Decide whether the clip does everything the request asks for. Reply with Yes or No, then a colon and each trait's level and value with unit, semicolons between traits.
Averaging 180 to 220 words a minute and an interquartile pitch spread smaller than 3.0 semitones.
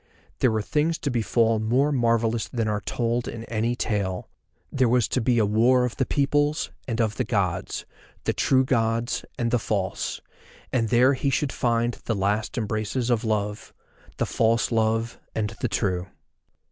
No: average, 170 wpm; narrow, 2.4 semitones